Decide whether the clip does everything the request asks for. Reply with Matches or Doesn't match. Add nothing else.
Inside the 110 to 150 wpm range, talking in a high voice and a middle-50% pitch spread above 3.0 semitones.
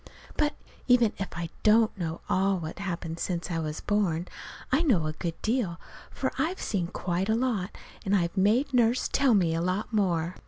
Doesn't match